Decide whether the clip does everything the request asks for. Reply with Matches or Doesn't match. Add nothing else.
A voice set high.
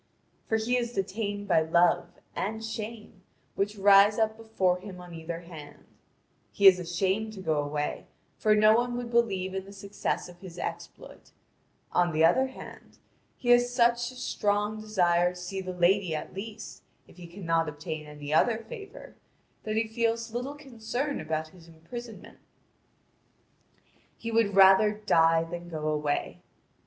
Matches